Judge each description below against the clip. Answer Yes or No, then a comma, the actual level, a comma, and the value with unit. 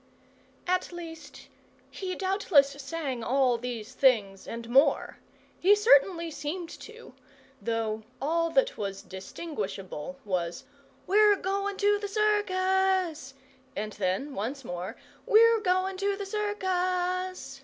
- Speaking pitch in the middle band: No, very high, 330 Hz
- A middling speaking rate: No, slow, 115 wpm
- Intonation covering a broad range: Yes, wide, 8.0 semitones